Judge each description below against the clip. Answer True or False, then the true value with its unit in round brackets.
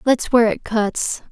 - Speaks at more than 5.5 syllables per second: False (4.4 syllables/s)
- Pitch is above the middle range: True (230 Hz)